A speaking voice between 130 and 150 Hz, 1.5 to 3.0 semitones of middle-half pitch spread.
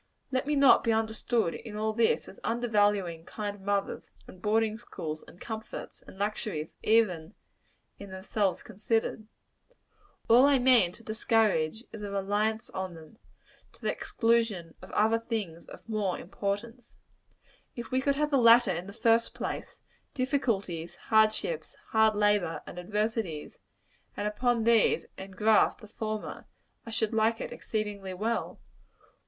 No: high, 215 Hz; narrow, 2.6 semitones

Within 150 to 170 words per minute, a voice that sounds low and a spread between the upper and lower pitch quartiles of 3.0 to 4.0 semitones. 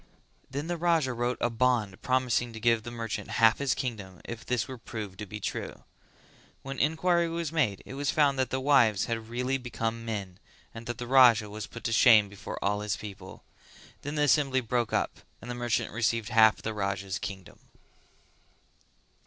No: average, 185 wpm; low, 120 Hz; average, 3.6 semitones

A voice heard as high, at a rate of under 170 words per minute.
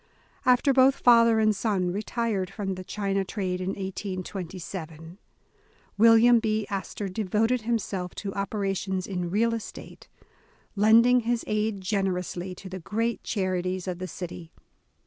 Yes: high, 195 Hz; average, 140 wpm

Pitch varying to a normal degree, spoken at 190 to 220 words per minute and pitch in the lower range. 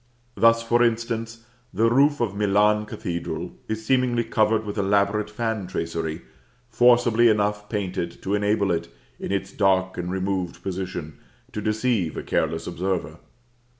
No: average, 3.5 semitones; average, 140 wpm; low, 105 Hz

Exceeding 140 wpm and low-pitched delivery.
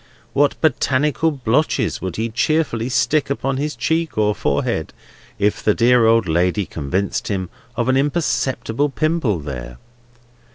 No: slow, 135 wpm; low, 120 Hz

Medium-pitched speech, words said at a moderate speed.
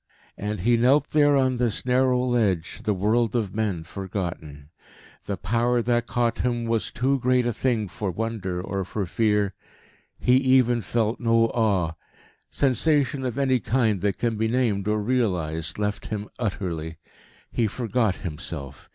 No: low, 110 Hz; average, 155 wpm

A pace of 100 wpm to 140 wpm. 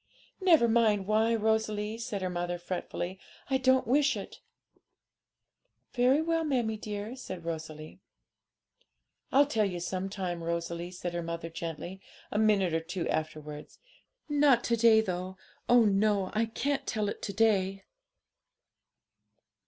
Yes: slow, 135 wpm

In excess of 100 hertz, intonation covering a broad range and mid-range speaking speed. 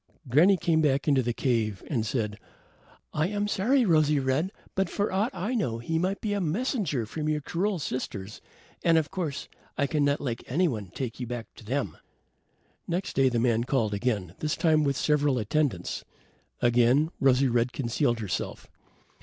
Yes: medium, 140 Hz; wide, 5.7 semitones; average, 170 wpm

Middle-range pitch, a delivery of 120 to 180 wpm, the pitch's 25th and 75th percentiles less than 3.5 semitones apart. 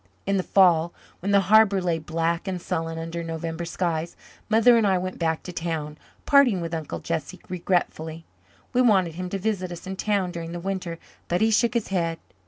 No: medium, 175 Hz; average, 195 wpm; average, 2.9 semitones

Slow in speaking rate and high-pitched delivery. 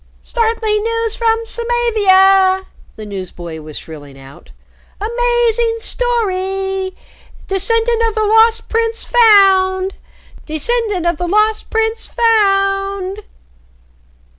Yes: slow, 95 wpm; very high, 420 Hz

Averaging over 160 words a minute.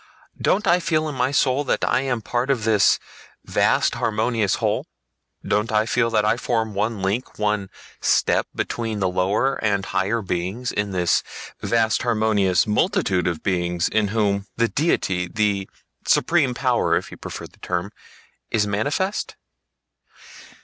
No: average, 145 wpm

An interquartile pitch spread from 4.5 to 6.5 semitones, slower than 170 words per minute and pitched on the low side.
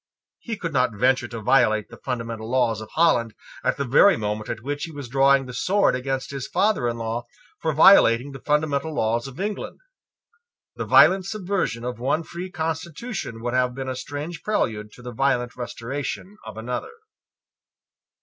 No: average, 5.1 semitones; average, 175 wpm; low, 130 Hz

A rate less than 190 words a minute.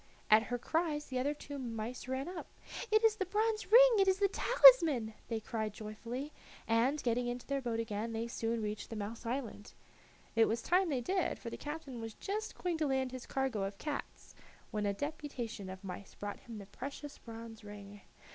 No: average, 200 wpm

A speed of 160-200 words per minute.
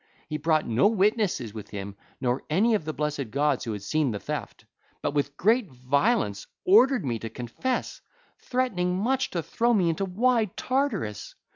Yes: average, 170 wpm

